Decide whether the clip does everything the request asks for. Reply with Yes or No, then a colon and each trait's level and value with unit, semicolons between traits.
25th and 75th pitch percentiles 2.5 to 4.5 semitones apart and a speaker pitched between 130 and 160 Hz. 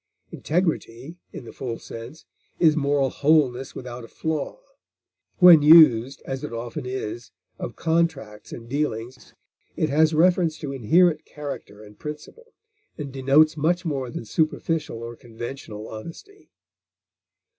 No: average, 5.0 semitones; medium, 140 Hz